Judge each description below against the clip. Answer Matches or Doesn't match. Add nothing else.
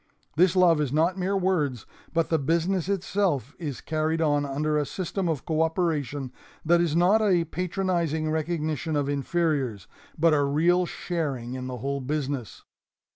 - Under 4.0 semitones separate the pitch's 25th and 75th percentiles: Matches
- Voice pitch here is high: Doesn't match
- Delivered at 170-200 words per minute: Doesn't match